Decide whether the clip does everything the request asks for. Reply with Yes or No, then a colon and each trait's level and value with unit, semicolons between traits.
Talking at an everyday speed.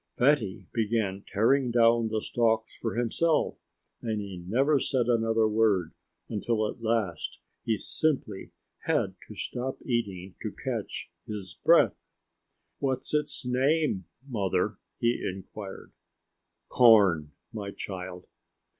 No: slow, 120 wpm